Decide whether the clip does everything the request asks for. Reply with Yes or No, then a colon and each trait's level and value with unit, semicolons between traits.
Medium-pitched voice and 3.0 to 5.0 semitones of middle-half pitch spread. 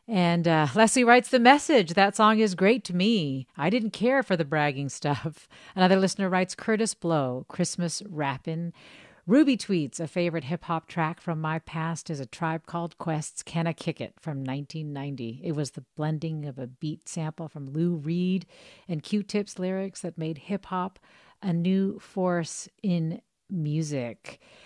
Yes: medium, 170 Hz; average, 3.7 semitones